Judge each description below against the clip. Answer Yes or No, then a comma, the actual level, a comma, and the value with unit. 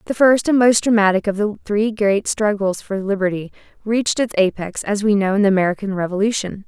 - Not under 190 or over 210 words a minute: Yes, average, 200 wpm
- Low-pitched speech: No, high, 205 Hz